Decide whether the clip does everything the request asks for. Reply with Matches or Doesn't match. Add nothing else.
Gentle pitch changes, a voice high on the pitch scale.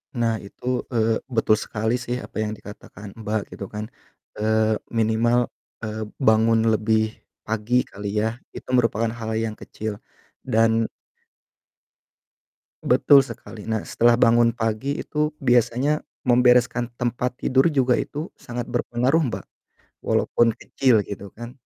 Doesn't match